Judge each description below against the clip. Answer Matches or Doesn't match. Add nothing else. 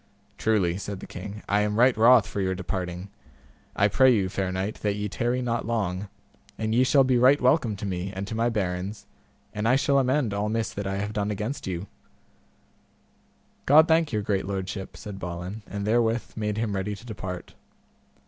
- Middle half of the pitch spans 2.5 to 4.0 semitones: Matches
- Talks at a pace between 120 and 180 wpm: Doesn't match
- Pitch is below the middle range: Matches